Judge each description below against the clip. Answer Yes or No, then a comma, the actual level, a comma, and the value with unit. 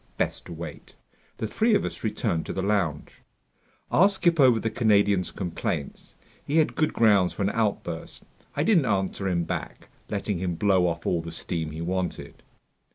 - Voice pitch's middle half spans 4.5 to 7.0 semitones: Yes, average, 4.9 semitones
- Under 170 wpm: No, average, 175 wpm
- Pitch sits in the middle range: No, low, 100 Hz